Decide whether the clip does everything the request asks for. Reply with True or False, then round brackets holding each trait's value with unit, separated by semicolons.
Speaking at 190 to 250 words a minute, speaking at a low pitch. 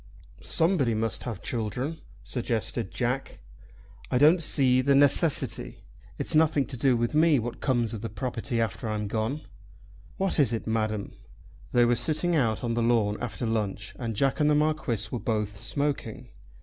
False (160 wpm; 120 Hz)